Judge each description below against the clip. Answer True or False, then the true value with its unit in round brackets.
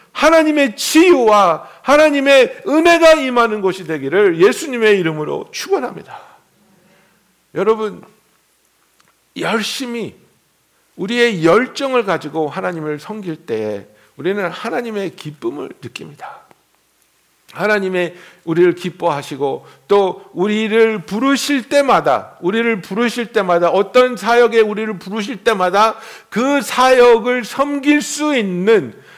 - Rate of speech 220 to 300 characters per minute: True (255 characters per minute)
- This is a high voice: True (220 Hz)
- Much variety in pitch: True (6.3 semitones)